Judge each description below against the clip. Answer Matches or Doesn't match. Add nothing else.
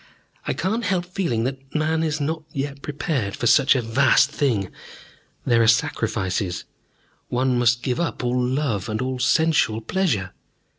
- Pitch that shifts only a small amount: Doesn't match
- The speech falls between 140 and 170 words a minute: Matches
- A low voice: Matches